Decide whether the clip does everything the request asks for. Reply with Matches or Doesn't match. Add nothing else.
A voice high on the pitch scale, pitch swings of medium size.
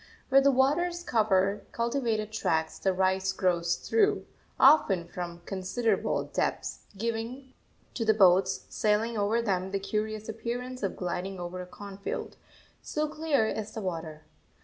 Matches